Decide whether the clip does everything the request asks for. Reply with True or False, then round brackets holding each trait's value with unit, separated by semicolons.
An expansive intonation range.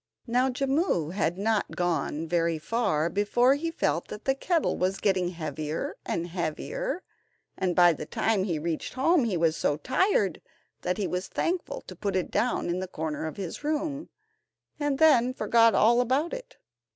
True (7.8 semitones)